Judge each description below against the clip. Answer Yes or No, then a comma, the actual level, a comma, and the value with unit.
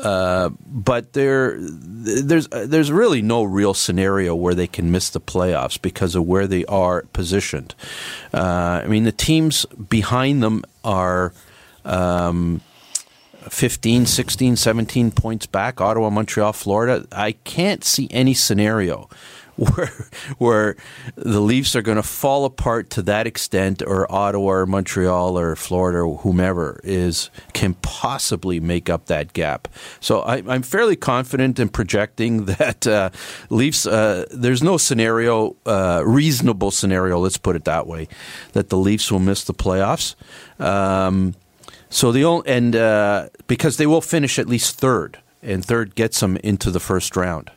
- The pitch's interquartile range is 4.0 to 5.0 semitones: Yes, average, 4.5 semitones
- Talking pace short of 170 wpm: Yes, average, 150 wpm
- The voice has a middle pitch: No, low, 105 Hz